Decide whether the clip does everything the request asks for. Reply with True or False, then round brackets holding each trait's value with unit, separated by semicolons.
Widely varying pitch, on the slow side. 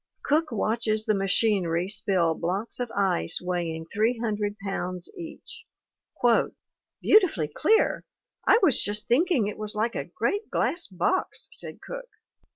True (6.8 semitones; 130 wpm)